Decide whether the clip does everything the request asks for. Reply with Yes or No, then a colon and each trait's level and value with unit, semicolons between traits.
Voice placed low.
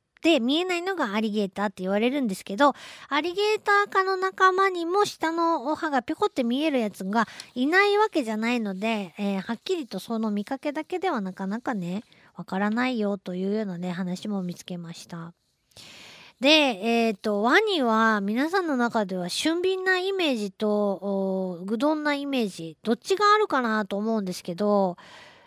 No: high, 230 Hz